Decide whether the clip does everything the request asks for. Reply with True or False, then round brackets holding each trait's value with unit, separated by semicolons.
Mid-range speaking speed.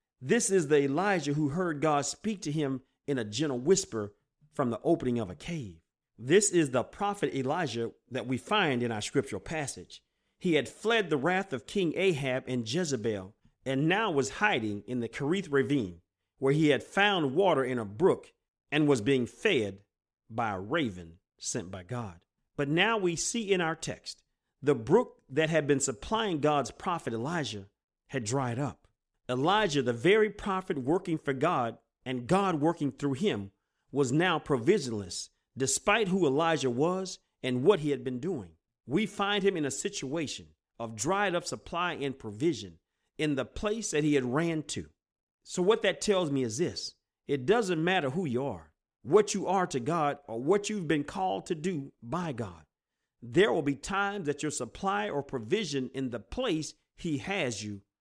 True (180 wpm)